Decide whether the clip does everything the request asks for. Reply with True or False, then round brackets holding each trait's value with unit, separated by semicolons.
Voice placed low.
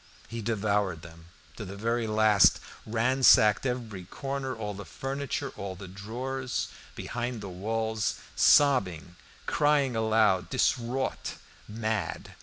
True (110 Hz)